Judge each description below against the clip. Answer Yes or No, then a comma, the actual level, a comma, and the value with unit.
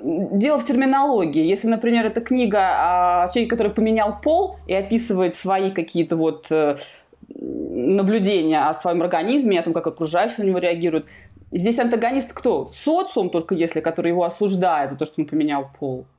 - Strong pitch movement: Yes, wide, 5.9 semitones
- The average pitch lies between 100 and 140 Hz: No, high, 190 Hz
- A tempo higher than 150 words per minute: Yes, fast, 160 wpm